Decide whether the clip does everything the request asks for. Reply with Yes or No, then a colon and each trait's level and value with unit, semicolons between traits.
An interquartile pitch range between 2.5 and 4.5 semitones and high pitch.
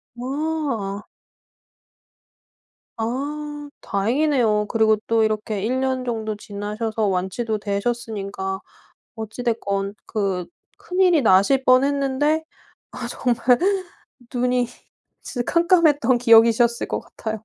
Yes: average, 4.0 semitones; high, 235 Hz